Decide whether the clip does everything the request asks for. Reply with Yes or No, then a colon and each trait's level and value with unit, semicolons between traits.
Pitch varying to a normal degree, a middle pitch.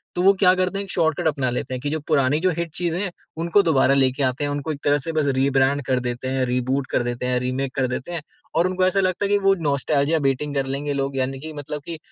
Yes: average, 4.3 semitones; medium, 145 Hz